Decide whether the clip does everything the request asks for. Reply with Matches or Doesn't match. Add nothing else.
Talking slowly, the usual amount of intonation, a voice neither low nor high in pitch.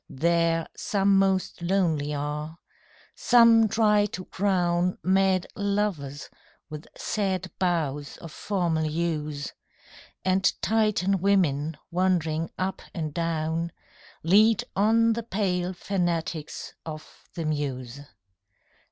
Matches